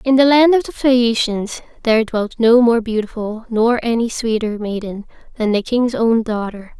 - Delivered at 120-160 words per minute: No, average, 175 wpm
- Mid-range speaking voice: No, high, 230 Hz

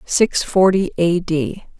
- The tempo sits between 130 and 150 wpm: Yes, slow, 135 wpm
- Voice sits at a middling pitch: Yes, medium, 180 Hz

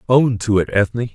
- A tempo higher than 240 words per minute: No, fast, 210 wpm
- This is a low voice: Yes, low, 115 Hz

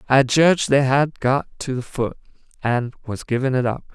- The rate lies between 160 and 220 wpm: Yes, average, 200 wpm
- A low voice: Yes, low, 130 Hz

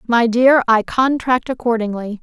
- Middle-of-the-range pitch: No, high, 235 Hz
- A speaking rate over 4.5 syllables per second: No, 4.4 syllables/s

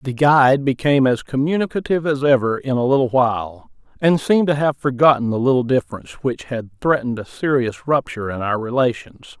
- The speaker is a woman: No, male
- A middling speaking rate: Yes, average, 180 wpm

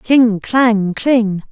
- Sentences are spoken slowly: Yes, slow, 120 wpm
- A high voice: Yes, high, 225 Hz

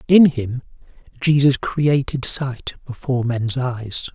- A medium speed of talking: No, slow, 115 wpm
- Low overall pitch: Yes, low, 130 Hz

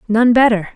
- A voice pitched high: Yes, high, 225 Hz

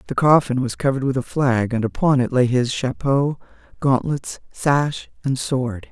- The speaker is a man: No, female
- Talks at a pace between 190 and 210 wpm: No, average, 175 wpm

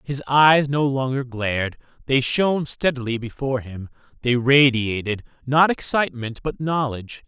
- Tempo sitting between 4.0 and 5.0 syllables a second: Yes, 4.8 syllables/s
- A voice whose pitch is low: Yes, low, 130 Hz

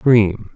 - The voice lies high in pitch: No, low, 110 Hz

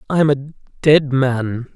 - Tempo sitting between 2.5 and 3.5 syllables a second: Yes, 3.3 syllables/s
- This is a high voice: No, low, 135 Hz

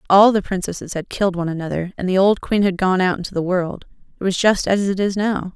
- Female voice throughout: Yes, female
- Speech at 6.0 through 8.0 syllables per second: Yes, 6.1 syllables/s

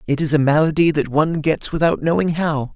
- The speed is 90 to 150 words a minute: No, fast, 220 wpm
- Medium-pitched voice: Yes, medium, 155 Hz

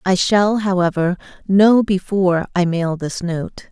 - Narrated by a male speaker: No, female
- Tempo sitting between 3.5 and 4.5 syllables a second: Yes, 4.0 syllables/s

